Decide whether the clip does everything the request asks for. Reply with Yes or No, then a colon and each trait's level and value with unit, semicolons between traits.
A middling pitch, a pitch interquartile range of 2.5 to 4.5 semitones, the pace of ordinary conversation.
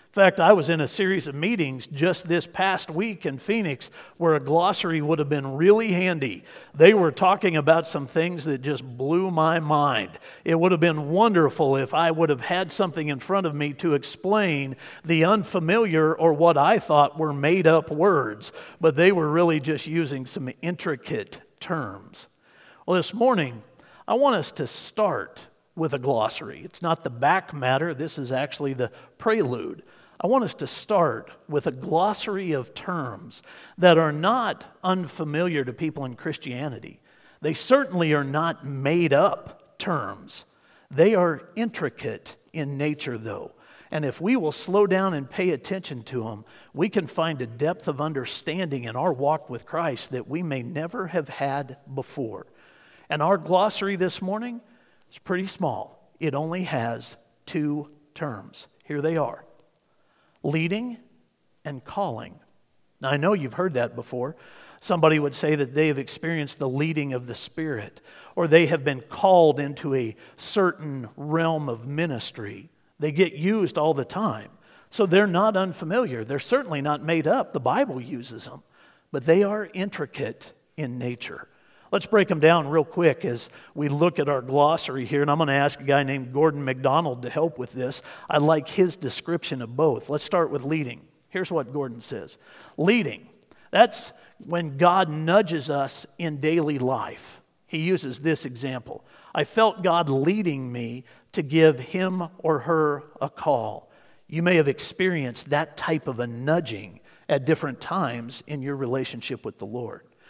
Yes: medium, 155 Hz; average, 4.2 semitones; average, 170 wpm